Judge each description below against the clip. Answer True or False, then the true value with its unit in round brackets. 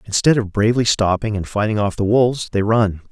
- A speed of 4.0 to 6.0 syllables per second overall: True (5.9 syllables/s)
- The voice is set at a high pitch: False (105 Hz)